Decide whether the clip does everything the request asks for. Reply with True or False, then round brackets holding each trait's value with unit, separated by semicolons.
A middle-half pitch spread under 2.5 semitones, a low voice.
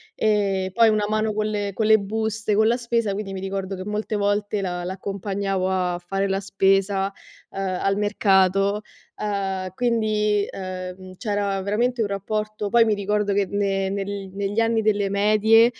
False (1.7 semitones; 200 Hz)